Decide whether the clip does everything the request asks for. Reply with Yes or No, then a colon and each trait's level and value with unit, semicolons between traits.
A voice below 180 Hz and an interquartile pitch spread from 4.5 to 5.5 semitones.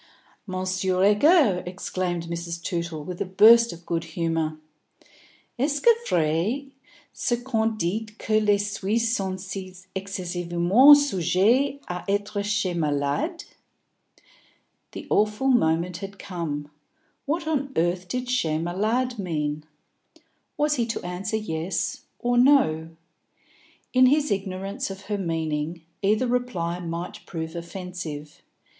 No: high, 190 Hz; average, 5.2 semitones